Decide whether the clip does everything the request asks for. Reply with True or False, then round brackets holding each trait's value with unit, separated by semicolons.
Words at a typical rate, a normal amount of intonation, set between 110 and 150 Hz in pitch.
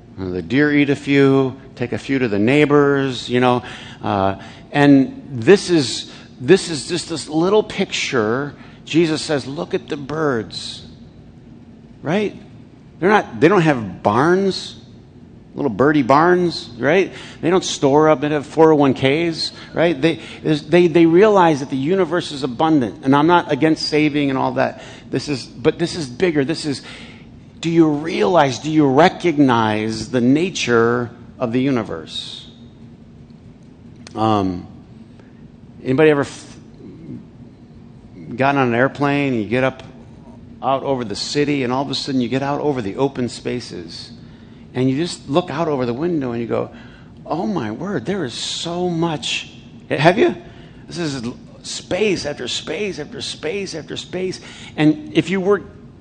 True (155 wpm; 4.5 semitones; 140 Hz)